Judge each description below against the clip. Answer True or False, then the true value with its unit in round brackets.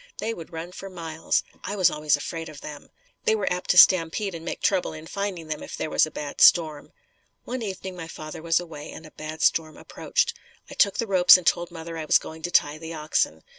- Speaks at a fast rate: True (230 wpm)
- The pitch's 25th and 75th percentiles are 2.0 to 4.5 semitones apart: True (2.9 semitones)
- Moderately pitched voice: True (165 Hz)